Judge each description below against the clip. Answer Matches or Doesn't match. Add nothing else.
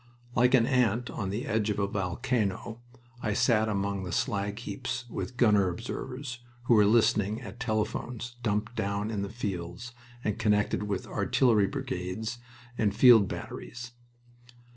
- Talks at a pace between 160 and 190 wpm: Doesn't match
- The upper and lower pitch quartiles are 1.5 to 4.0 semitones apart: Matches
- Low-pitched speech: Matches